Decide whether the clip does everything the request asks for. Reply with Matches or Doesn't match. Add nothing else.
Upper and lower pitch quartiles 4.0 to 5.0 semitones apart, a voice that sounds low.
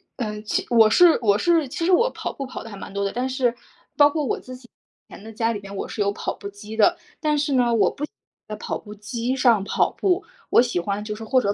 Doesn't match